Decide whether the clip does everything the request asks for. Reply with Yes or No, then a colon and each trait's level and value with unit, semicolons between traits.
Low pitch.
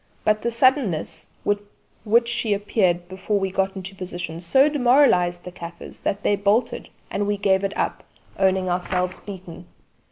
No: high, 195 Hz